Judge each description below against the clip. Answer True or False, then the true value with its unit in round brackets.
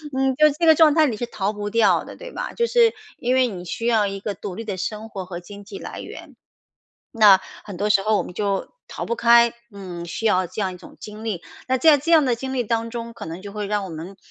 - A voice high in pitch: True (215 Hz)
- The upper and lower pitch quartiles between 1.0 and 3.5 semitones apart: False (3.9 semitones)